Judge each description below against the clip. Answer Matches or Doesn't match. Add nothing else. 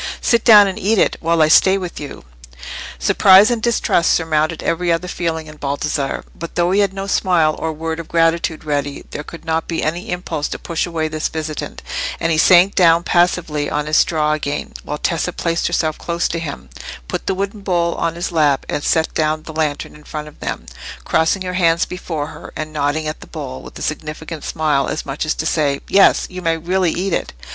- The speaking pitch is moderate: Matches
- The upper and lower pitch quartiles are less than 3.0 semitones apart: Matches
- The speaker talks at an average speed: Doesn't match